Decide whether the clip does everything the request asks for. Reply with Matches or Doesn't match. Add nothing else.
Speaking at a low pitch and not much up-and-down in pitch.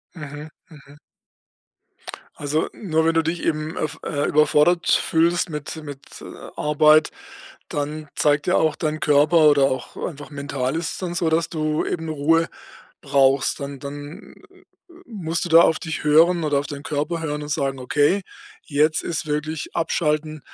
Doesn't match